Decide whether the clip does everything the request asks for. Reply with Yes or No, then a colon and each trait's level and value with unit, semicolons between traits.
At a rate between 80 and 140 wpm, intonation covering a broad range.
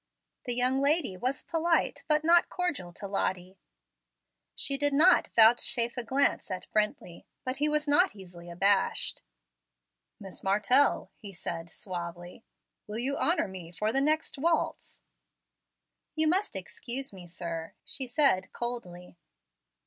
Yes: slow, 135 wpm; wide, 7.6 semitones